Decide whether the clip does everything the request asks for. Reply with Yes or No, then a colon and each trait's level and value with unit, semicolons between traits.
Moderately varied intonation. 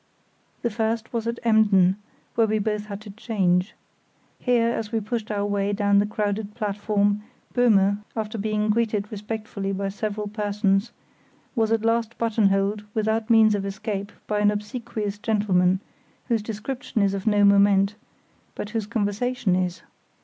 No: narrow, 1.8 semitones